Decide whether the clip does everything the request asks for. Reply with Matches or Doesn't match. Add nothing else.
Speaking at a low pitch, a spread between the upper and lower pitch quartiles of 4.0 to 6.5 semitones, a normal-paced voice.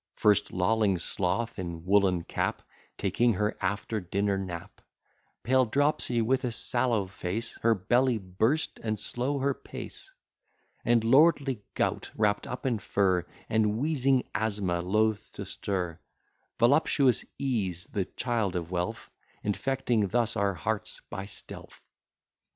Doesn't match